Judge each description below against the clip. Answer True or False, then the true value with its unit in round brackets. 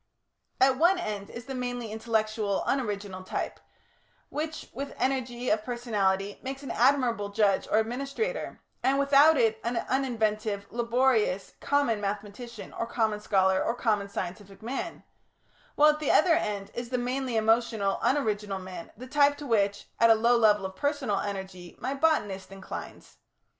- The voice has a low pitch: False (230 Hz)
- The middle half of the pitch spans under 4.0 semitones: False (4.5 semitones)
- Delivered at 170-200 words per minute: False (155 wpm)